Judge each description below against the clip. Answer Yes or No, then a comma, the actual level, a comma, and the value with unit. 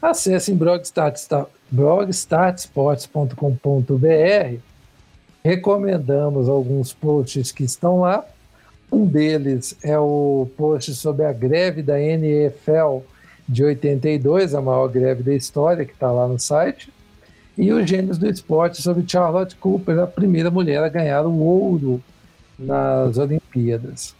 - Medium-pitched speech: Yes, medium, 150 Hz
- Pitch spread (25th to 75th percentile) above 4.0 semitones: Yes, average, 4.5 semitones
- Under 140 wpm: Yes, average, 125 wpm